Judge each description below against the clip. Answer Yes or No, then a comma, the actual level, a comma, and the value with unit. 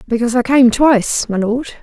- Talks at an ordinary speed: Yes, average, 195 wpm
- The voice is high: Yes, high, 240 Hz